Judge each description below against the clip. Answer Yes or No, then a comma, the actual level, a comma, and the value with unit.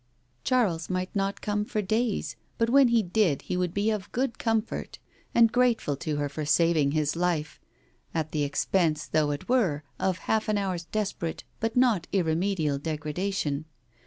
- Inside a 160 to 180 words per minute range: Yes, average, 165 wpm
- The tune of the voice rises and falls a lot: Yes, wide, 5.7 semitones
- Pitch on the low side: No, medium, 185 Hz